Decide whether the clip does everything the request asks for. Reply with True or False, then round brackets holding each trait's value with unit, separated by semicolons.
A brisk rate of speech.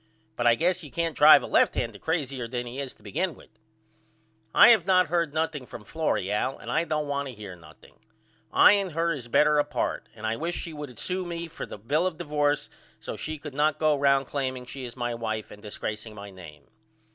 True (225 wpm)